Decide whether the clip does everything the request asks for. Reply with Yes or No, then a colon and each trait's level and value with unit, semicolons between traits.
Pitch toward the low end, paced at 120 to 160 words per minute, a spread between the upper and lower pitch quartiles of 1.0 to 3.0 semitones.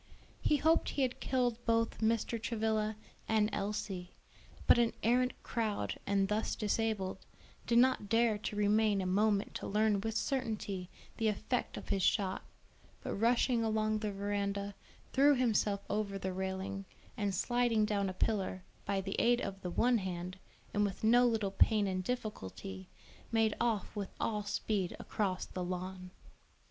No: high, 210 Hz; average, 155 wpm; average, 2.7 semitones